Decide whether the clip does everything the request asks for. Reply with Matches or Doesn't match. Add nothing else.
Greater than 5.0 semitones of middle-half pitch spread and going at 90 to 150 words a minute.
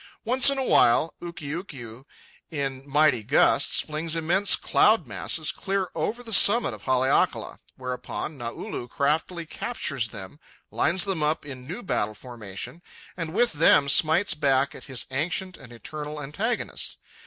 Matches